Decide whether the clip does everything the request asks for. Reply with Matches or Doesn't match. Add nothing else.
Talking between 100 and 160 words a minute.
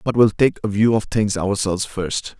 Doesn't match